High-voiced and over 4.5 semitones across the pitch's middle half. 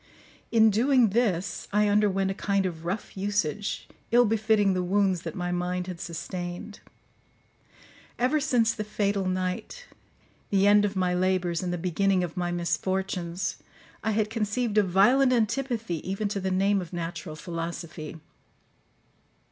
No: high, 195 Hz; average, 3.0 semitones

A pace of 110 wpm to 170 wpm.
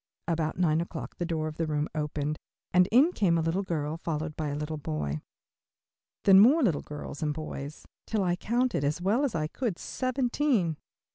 No: average, 190 wpm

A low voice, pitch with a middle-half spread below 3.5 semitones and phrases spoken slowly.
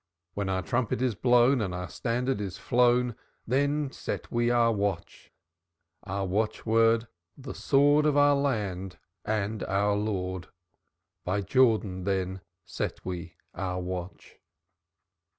No: low, 105 Hz; average, 4.8 semitones; slow, 125 wpm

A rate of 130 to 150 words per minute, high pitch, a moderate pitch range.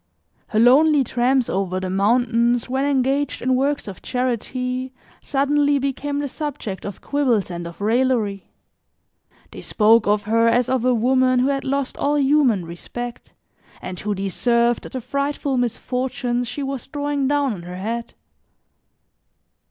Yes: average, 145 wpm; very high, 250 Hz; average, 3.7 semitones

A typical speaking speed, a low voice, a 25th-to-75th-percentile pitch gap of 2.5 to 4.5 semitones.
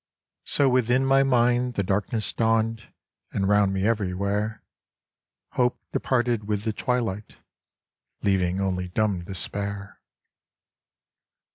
No: slow, 105 wpm; low, 105 Hz; average, 3.6 semitones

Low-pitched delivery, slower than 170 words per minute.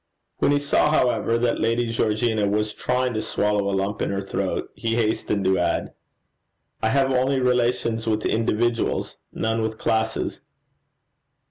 Yes: low, 115 Hz; average, 150 wpm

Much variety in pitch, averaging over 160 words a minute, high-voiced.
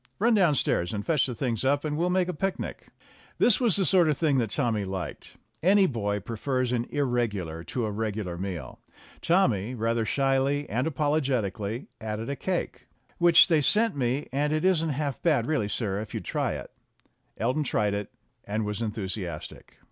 No: wide, 6.4 semitones; average, 180 wpm; low, 130 Hz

